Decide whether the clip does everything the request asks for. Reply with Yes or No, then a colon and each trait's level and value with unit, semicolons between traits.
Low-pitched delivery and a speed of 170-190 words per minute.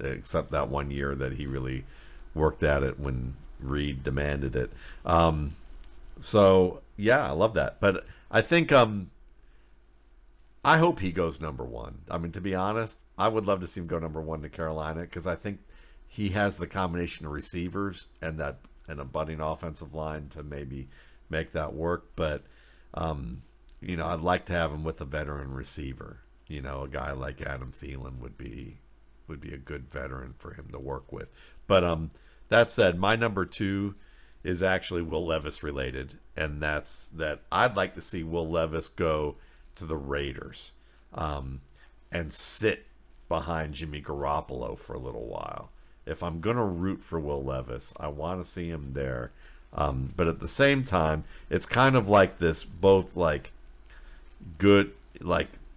Yes: very low, 80 Hz; average, 175 wpm